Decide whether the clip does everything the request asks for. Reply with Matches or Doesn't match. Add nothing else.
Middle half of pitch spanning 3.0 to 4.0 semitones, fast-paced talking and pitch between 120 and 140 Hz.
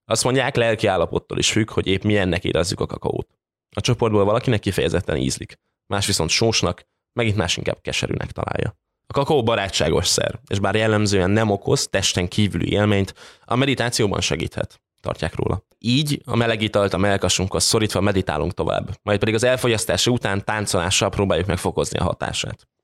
Doesn't match